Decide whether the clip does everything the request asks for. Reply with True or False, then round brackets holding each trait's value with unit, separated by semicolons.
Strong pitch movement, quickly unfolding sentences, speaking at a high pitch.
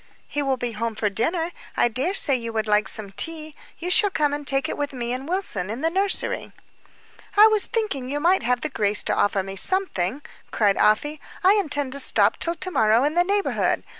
True (7.4 semitones; 220 wpm; 280 Hz)